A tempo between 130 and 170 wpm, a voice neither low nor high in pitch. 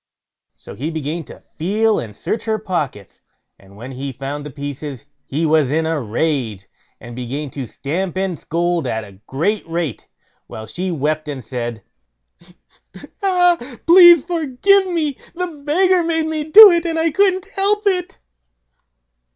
Yes: average, 155 wpm; medium, 170 Hz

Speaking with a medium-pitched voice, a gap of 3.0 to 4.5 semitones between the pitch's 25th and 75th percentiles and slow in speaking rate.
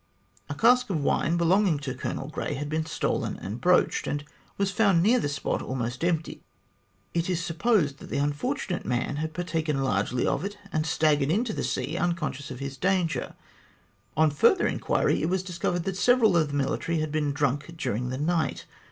No: medium, 160 Hz; average, 3.9 semitones; average, 185 wpm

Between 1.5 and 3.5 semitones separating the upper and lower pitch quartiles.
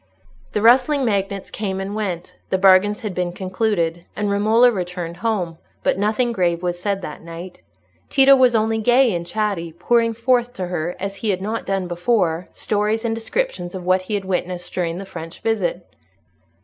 No: average, 3.9 semitones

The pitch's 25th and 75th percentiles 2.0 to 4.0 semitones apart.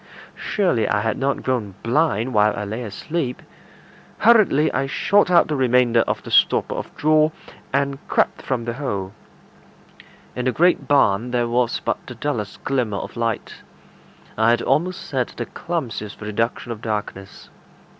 No: average, 4.6 semitones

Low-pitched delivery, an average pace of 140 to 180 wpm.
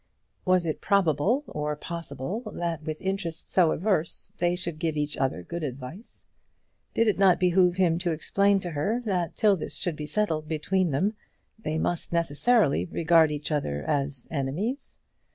No: medium, 170 Hz; average, 165 wpm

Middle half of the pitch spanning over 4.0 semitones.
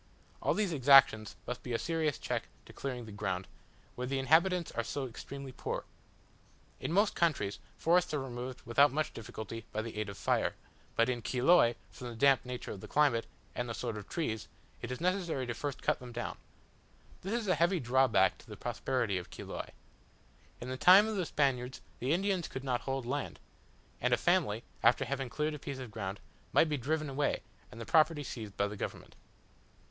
Yes: average, 4.7 semitones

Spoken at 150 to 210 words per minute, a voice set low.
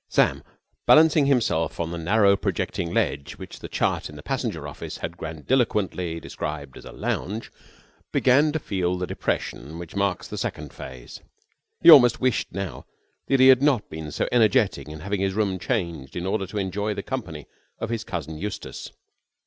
Yes: average, 175 wpm; very low, 95 Hz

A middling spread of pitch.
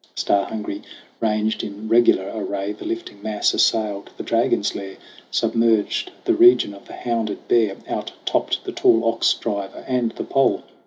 No: narrow, 2.2 semitones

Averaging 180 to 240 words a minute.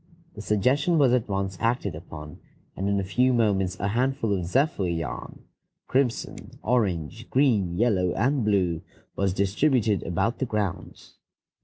No: average, 145 wpm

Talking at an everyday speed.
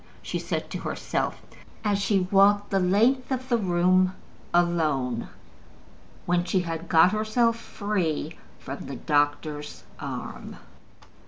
No: slow, 120 wpm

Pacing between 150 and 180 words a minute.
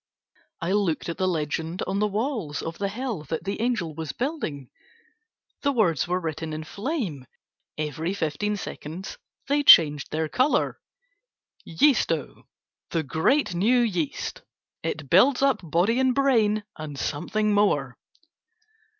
No: slow, 135 wpm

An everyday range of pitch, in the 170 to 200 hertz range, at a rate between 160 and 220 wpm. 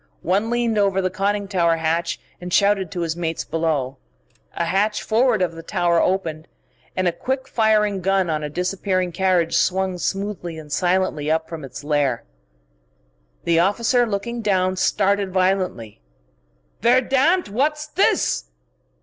No: average, 3.7 semitones; medium, 185 Hz; average, 150 wpm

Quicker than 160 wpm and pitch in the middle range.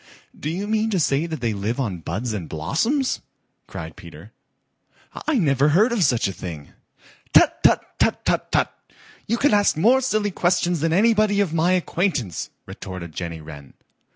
Yes: average, 170 wpm; medium, 160 Hz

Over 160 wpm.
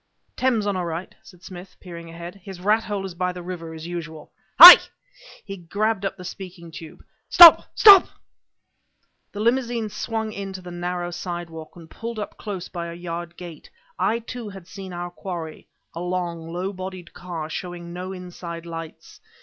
Yes: average, 175 wpm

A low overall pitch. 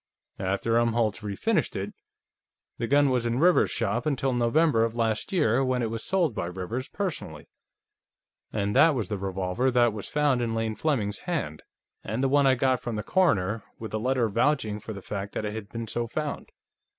Yes: low, 115 Hz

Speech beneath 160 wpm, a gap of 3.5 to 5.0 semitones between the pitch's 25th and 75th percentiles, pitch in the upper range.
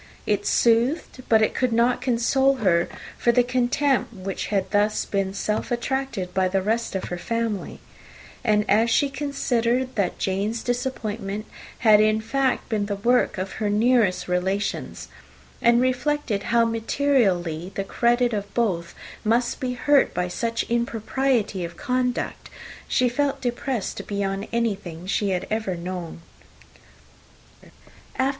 Yes: average, 140 wpm; average, 4.0 semitones; high, 225 Hz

